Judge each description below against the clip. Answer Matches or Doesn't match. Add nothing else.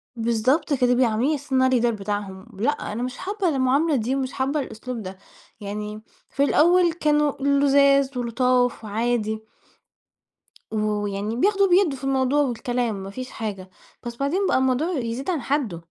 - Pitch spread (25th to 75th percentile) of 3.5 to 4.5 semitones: Matches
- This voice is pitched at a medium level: Doesn't match